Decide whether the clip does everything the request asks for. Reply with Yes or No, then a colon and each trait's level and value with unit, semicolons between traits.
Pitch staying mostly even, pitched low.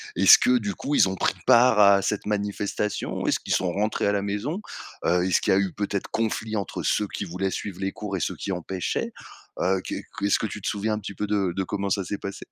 Yes: narrow, 1.6 semitones; low, 100 Hz